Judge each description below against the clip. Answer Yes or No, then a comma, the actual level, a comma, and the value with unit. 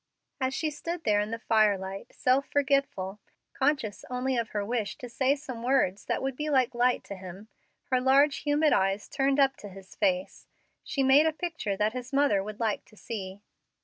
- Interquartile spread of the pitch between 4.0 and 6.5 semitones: Yes, average, 5.0 semitones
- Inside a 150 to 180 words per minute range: No, average, 195 wpm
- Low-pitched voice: No, very high, 250 Hz